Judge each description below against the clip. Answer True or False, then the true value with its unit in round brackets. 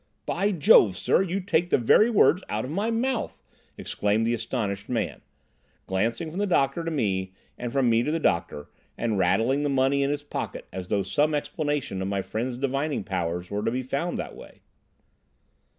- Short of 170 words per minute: False (190 wpm)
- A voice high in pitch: False (130 Hz)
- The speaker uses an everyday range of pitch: False (7.4 semitones)